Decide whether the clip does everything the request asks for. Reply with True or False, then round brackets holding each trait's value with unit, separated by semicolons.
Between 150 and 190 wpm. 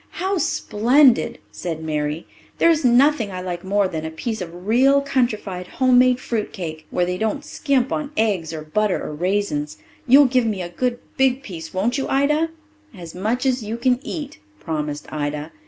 True (180 wpm)